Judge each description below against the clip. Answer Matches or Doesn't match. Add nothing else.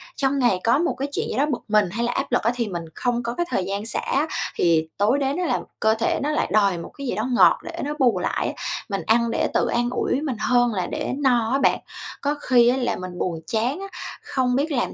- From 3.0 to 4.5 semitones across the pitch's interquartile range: Matches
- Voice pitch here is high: Matches